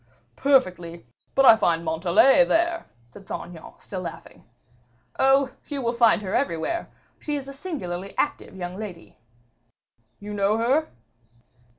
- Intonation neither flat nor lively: No, wide, 7.5 semitones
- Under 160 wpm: Yes, slow, 135 wpm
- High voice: Yes, high, 215 Hz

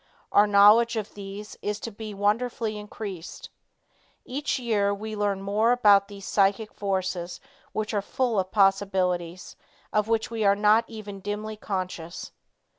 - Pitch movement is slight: Yes, narrow, 1.8 semitones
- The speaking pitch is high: Yes, high, 205 Hz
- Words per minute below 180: Yes, average, 145 wpm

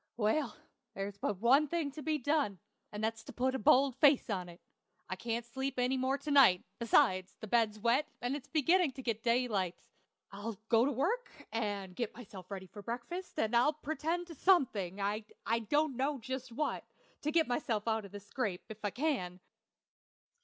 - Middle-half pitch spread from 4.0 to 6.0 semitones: Yes, wide, 5.4 semitones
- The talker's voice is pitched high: Yes, high, 240 Hz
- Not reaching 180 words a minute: No, average, 190 wpm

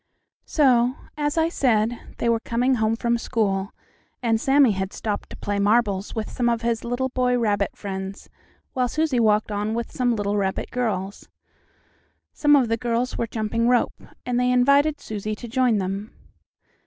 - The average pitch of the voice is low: No, high, 230 Hz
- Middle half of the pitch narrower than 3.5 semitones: Yes, average, 3.0 semitones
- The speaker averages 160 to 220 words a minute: Yes, average, 170 wpm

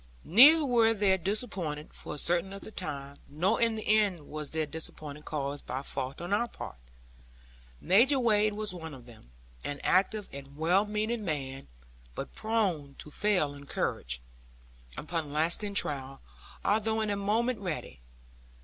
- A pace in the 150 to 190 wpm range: Yes, average, 160 wpm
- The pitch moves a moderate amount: No, wide, 6.6 semitones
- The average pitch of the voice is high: No, medium, 180 Hz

